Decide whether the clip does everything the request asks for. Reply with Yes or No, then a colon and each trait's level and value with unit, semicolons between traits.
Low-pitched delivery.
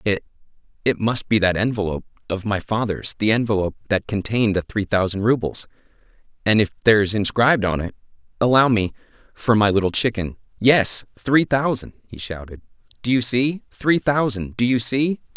Yes: low, 110 Hz